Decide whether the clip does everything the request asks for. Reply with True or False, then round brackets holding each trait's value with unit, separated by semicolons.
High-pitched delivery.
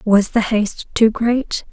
True (220 Hz)